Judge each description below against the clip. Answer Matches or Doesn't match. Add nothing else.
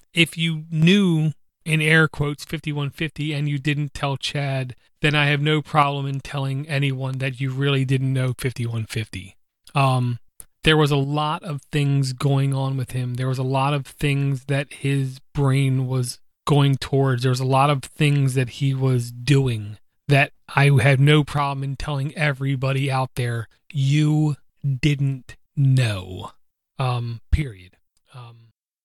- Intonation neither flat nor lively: Doesn't match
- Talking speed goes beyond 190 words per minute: Doesn't match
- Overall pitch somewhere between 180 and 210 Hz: Doesn't match